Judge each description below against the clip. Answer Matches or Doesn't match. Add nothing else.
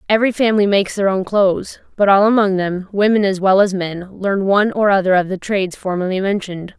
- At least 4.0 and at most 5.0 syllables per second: Doesn't match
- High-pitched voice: Matches